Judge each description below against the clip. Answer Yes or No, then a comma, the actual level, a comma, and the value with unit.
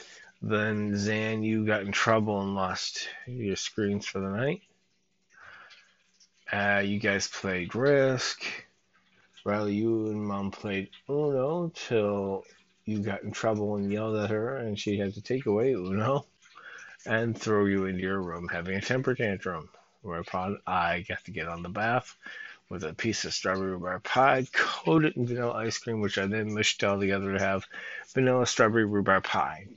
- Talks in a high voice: No, low, 105 Hz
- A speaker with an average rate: Yes, average, 165 wpm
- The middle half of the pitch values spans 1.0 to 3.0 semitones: Yes, narrow, 2.5 semitones